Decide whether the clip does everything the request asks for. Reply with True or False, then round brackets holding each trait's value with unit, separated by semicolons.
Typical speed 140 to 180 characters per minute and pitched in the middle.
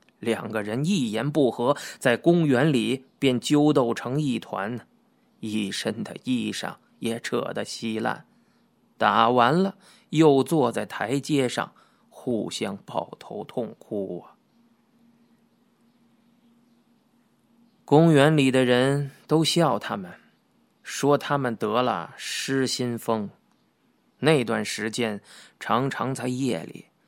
True (155 characters per minute; 145 Hz)